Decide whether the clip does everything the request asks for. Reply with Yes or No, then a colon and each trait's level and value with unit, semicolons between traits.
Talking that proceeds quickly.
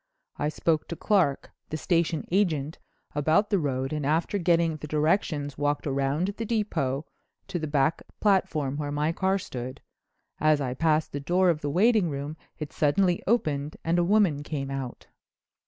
No: average, 170 wpm